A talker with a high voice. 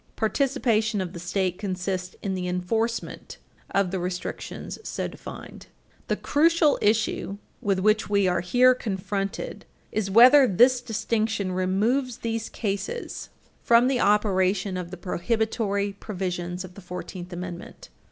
Yes: high, 200 Hz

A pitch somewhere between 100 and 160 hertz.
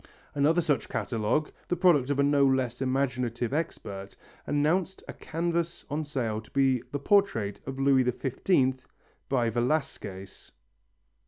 Yes: low, 135 Hz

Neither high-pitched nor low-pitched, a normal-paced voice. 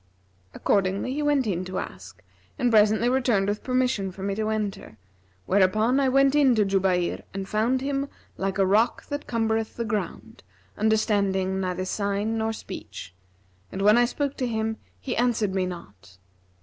No: high, 215 Hz; average, 165 wpm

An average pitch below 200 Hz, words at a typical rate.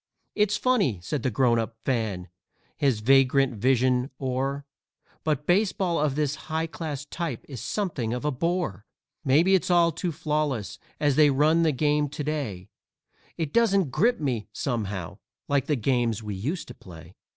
Yes: medium, 140 Hz; average, 160 wpm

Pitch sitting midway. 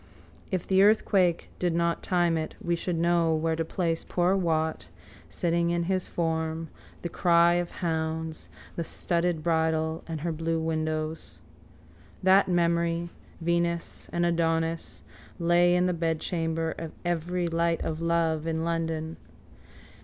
Yes: medium, 170 Hz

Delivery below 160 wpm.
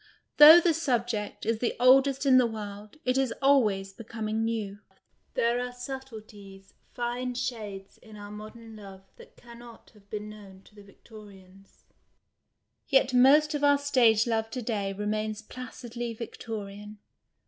Yes: average, 150 wpm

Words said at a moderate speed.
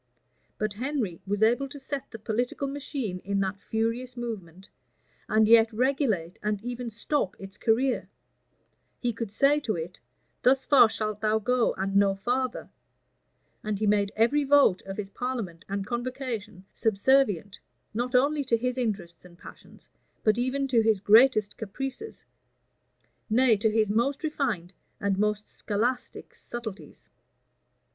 Yes: average, 145 wpm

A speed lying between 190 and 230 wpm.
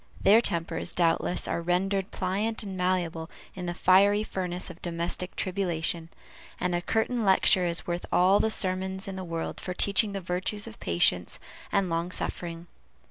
No: average, 165 wpm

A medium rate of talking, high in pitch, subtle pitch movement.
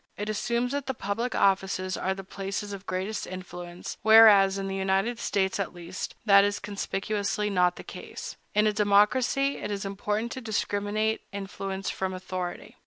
Yes: average, 170 wpm; high, 200 Hz; narrow, 1.9 semitones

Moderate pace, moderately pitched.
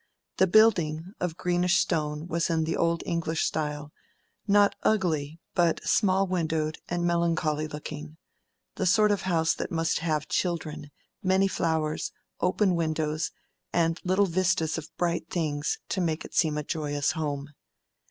Yes: average, 145 wpm; medium, 165 Hz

